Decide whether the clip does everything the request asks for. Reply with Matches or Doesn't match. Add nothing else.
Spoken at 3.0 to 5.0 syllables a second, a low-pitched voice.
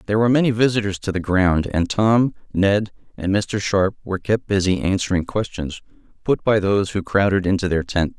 Doesn't match